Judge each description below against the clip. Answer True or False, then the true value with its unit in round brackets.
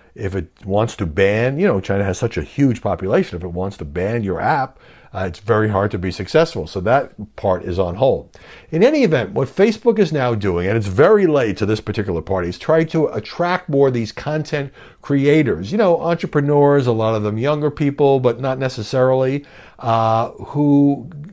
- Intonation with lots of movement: True (6.8 semitones)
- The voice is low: True (120 Hz)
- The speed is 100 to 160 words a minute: False (205 wpm)